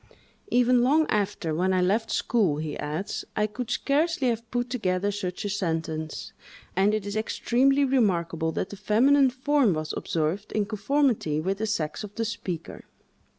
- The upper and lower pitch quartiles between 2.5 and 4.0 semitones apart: No, average, 5.3 semitones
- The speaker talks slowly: No, average, 165 wpm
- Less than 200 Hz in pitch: No, high, 210 Hz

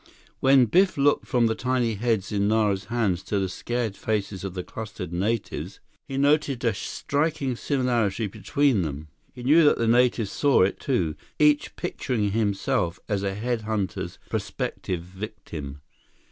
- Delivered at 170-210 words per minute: No, average, 155 wpm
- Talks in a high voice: No, low, 110 Hz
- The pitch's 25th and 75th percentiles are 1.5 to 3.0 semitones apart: No, average, 4.6 semitones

